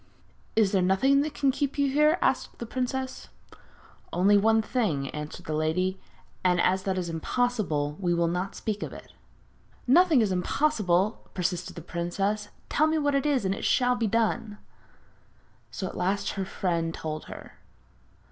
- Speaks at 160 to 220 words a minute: Yes, average, 165 wpm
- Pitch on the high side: Yes, high, 200 Hz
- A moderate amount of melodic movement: No, wide, 6.1 semitones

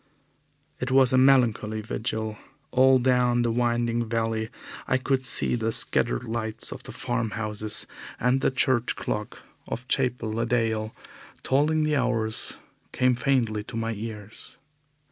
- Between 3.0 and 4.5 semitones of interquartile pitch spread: No, narrow, 2.5 semitones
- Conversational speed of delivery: Yes, average, 145 wpm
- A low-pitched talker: Yes, low, 120 Hz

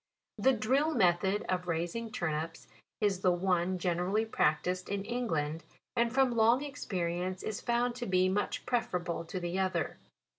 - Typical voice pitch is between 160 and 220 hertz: Yes, medium, 185 Hz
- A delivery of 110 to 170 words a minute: Yes, average, 155 wpm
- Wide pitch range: No, average, 4.9 semitones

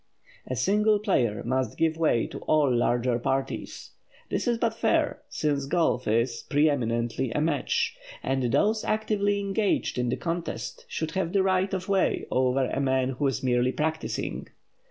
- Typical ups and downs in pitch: No, wide, 7.0 semitones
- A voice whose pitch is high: No, medium, 145 Hz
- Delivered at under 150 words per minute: No, average, 160 wpm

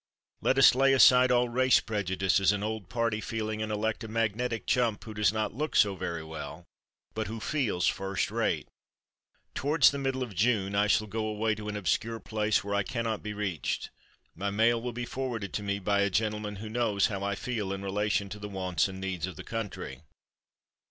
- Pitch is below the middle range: Yes, low, 105 Hz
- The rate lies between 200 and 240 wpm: Yes, fast, 205 wpm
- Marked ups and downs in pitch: No, narrow, 2.6 semitones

